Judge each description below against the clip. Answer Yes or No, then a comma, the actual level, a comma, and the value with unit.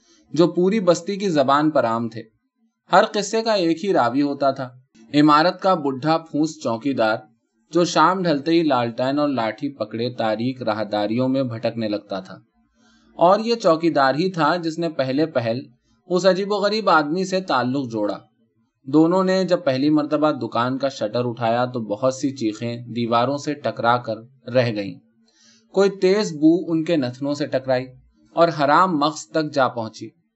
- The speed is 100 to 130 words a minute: No, average, 170 wpm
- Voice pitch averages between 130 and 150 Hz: Yes, medium, 140 Hz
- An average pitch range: No, wide, 6.2 semitones